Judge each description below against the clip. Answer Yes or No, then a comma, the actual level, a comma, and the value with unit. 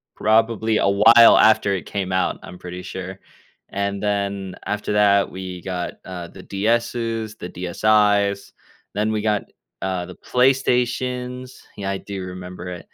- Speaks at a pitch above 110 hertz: No, low, 100 Hz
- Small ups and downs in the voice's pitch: No, average, 3.0 semitones